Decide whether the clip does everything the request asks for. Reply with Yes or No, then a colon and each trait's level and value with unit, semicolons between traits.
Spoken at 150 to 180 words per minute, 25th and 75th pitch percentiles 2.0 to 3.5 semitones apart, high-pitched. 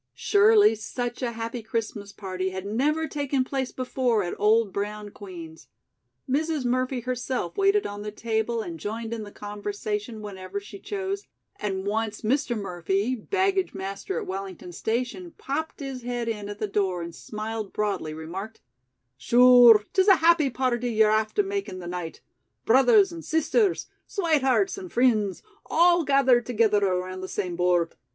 No: average, 155 wpm; average, 4.9 semitones; high, 225 Hz